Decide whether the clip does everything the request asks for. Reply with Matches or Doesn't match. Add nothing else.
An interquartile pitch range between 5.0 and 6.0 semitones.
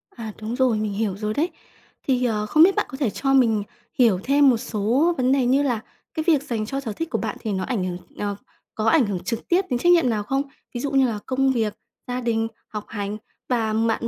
Doesn't match